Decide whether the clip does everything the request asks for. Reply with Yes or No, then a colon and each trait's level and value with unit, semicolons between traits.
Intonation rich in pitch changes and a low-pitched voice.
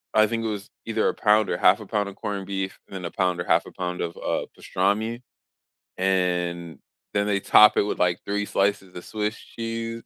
No: average, 2.8 semitones; low, 100 Hz